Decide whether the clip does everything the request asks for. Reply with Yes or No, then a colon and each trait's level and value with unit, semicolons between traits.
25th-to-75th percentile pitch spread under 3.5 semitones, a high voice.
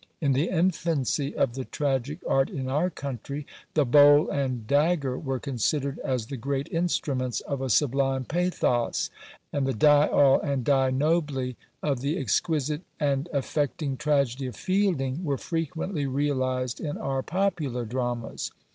No: narrow, 2.5 semitones; medium, 140 Hz